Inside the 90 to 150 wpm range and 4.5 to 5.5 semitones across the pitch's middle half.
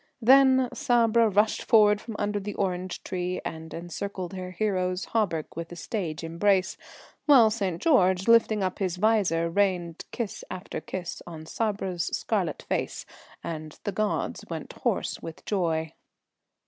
No: average, 145 wpm; average, 3.7 semitones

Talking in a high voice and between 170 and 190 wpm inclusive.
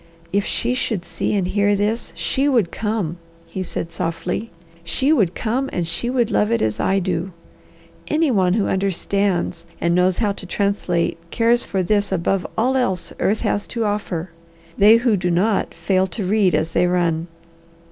Yes: high, 195 Hz; average, 180 wpm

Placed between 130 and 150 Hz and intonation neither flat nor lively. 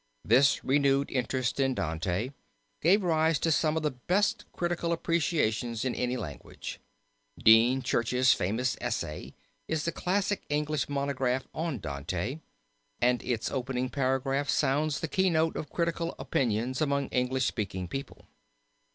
Yes: low, 135 Hz; average, 4.2 semitones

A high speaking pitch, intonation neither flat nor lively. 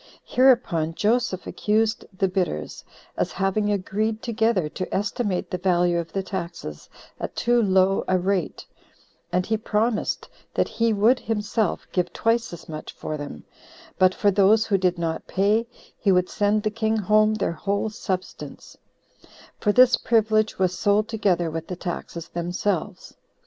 Yes: high, 200 Hz; average, 3.3 semitones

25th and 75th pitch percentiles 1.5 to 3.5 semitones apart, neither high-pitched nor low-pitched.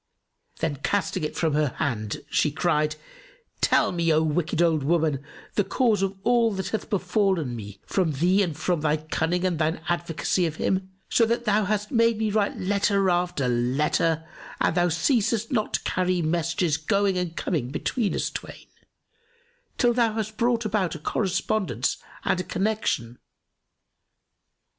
No: average, 4.7 semitones; medium, 180 Hz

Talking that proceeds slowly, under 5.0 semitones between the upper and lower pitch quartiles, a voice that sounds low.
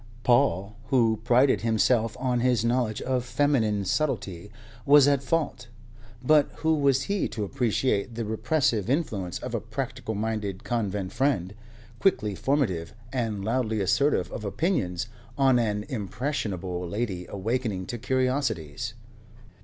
Yes: slow, 130 wpm; average, 4.4 semitones; low, 115 Hz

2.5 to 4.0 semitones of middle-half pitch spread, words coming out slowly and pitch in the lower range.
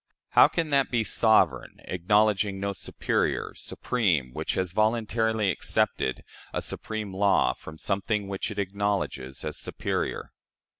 Yes: average, 2.8 semitones; slow, 130 wpm; low, 100 Hz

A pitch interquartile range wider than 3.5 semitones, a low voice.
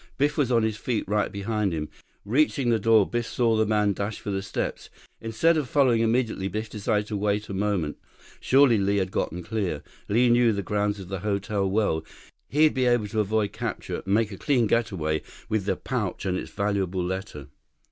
No: average, 2.9 semitones; low, 105 Hz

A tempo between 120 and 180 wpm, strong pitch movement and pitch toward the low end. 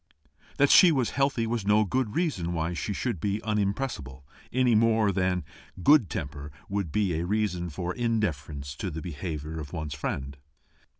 Yes: average, 165 wpm; wide, 6.2 semitones; very low, 95 Hz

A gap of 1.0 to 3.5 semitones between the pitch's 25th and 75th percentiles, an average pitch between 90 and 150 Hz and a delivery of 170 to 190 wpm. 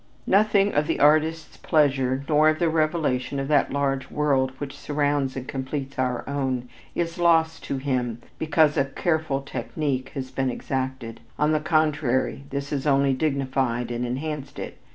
No: average, 2.8 semitones; medium, 140 Hz; average, 160 wpm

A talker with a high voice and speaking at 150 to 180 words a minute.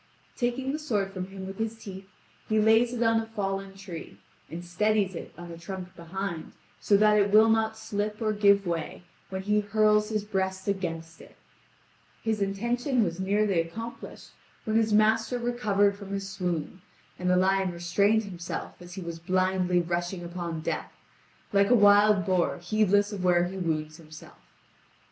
Yes: high, 195 Hz; average, 170 wpm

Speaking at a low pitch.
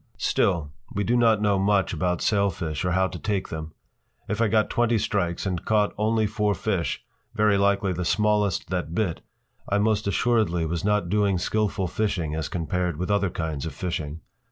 Yes: low, 100 Hz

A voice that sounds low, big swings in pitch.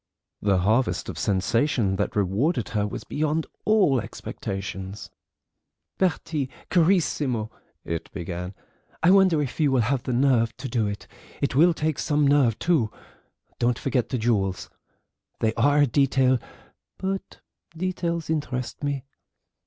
Yes: low, 130 Hz; wide, 6.1 semitones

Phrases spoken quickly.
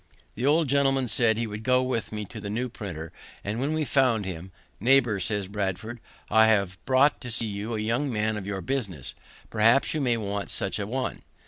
Yes: fast, 210 wpm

